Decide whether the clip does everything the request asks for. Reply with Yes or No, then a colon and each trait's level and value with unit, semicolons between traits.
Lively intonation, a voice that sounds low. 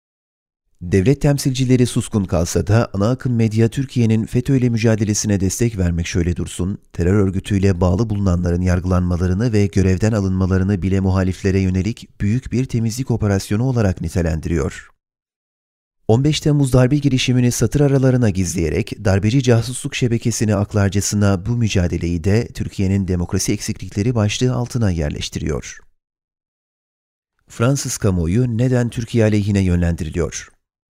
No: average, 4.5 semitones; low, 105 Hz